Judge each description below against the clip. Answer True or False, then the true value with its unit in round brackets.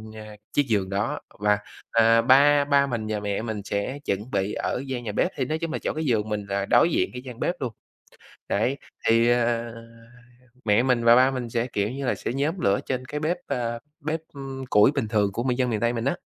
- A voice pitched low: True (120 Hz)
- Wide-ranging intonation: False (3.9 semitones)